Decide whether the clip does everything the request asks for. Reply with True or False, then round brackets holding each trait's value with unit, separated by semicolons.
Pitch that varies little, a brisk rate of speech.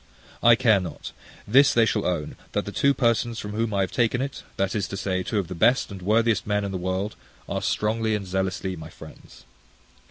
False (3.4 semitones; 220 wpm)